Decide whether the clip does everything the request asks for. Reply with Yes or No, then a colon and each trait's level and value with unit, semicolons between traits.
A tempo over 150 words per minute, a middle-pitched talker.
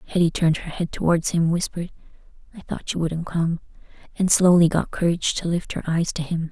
Yes: fast, 205 wpm; medium, 170 Hz